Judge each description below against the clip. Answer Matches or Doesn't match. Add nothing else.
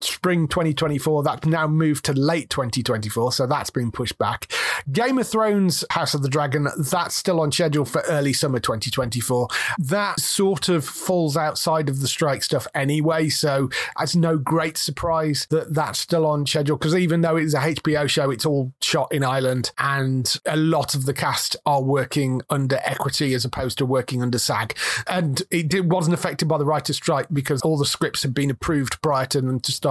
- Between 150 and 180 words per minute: Doesn't match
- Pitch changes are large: Doesn't match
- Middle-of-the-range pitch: Matches